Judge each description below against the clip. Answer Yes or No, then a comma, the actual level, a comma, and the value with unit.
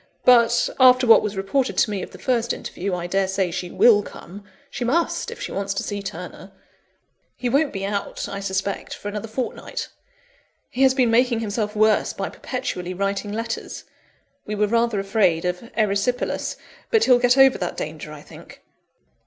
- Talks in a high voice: Yes, high, 210 Hz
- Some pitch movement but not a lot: Yes, average, 3.7 semitones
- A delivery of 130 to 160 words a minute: No, average, 175 wpm